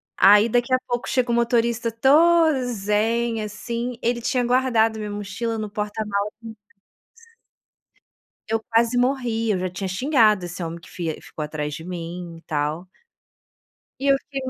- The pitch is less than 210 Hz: No, high, 225 Hz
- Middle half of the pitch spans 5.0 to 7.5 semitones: No, average, 3.9 semitones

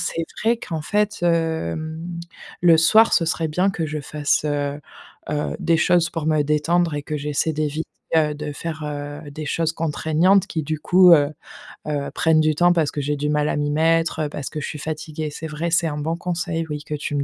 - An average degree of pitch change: No, narrow, 2.0 semitones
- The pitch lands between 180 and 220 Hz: No, medium, 155 Hz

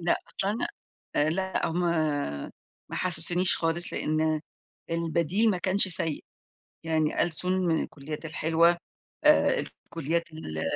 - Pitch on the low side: No, medium, 165 Hz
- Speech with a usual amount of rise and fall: No, narrow, 2.3 semitones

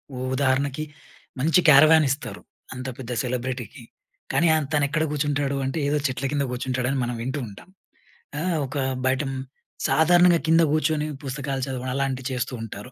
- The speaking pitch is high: No, medium, 140 Hz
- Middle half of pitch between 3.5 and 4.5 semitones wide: No, average, 3.1 semitones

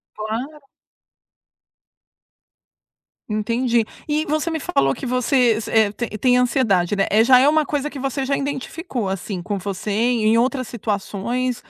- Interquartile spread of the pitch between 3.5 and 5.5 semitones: Yes, average, 4.2 semitones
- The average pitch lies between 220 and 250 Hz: Yes, high, 240 Hz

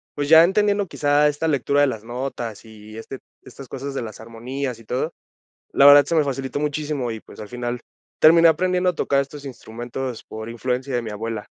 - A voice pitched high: No, low, 135 Hz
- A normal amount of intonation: Yes, average, 4.0 semitones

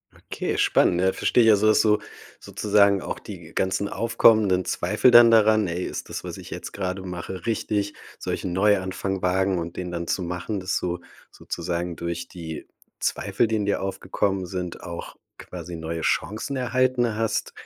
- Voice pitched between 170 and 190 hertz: No, very low, 95 Hz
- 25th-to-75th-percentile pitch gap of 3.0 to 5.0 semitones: Yes, average, 3.3 semitones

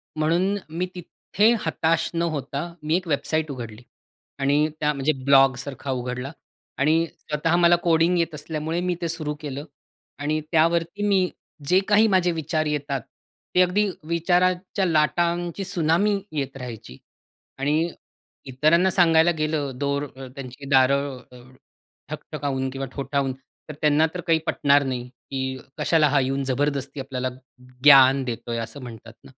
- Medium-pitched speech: Yes, medium, 150 Hz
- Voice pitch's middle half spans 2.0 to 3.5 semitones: No, average, 3.9 semitones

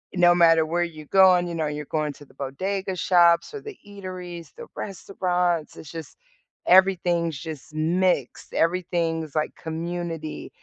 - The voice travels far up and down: No, narrow, 2.5 semitones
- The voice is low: No, medium, 170 Hz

